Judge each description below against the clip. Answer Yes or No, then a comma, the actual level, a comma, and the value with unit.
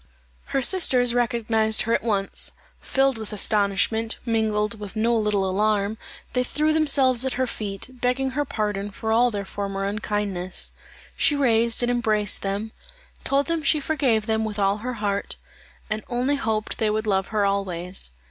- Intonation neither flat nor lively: Yes, average, 3.3 semitones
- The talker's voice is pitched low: No, high, 220 Hz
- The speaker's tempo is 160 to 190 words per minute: Yes, average, 165 wpm